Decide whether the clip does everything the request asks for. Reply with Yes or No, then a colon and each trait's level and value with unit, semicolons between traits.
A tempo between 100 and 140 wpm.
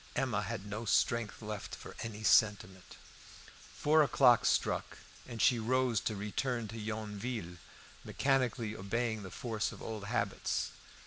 Yes: slow, 135 wpm